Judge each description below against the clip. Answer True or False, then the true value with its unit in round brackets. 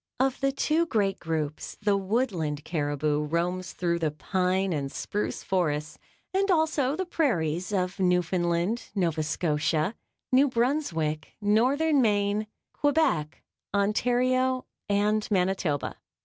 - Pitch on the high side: True (195 Hz)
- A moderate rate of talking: False (115 wpm)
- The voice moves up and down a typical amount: False (7.6 semitones)